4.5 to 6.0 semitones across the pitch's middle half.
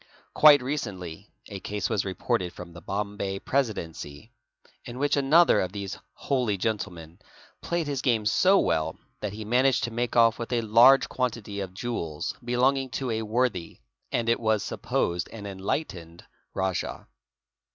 Yes: average, 4.9 semitones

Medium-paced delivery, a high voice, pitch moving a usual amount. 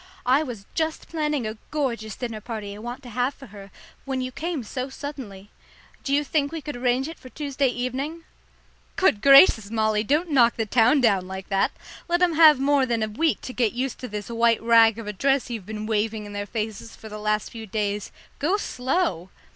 No: fast, 210 wpm; high, 245 Hz; average, 4.7 semitones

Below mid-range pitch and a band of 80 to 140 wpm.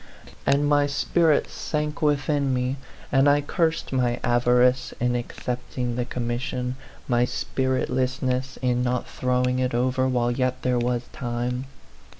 Yes: low, 125 Hz; slow, 135 wpm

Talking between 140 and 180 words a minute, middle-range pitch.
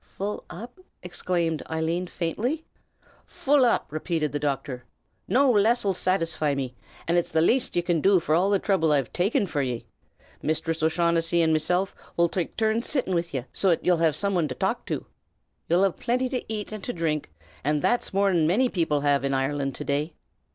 No: average, 195 wpm; medium, 170 Hz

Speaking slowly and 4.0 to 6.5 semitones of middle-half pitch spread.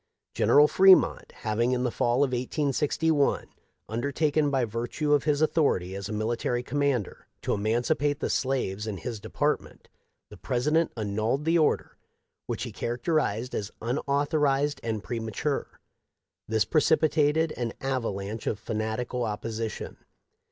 Yes: slow, 130 wpm; average, 4.7 semitones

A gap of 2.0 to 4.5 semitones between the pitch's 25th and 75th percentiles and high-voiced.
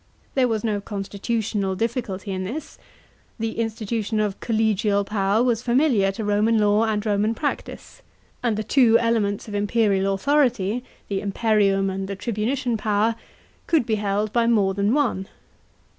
Yes: narrow, 2.4 semitones; high, 215 Hz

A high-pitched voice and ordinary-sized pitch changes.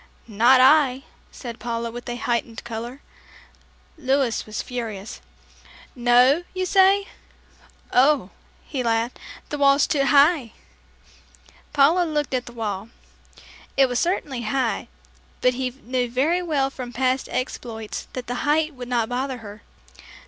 Yes: very high, 255 Hz; average, 3.0 semitones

